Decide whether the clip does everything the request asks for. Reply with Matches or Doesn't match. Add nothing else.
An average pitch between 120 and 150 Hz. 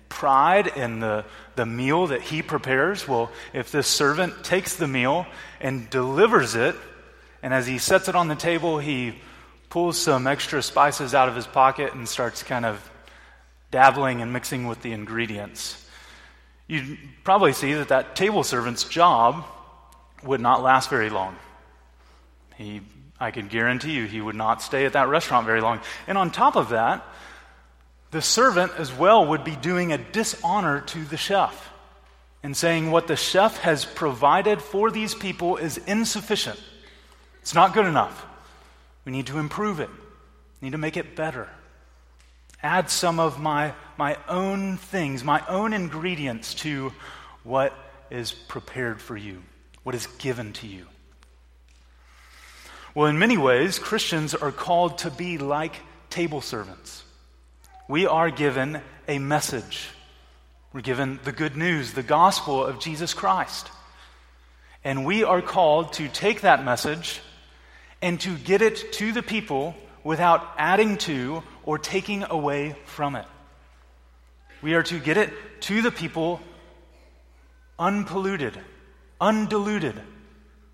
Matches